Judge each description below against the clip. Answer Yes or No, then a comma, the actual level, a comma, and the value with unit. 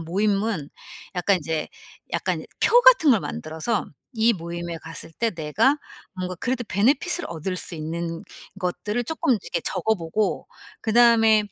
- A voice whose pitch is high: Yes, high, 195 Hz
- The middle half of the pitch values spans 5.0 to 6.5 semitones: Yes, wide, 5.6 semitones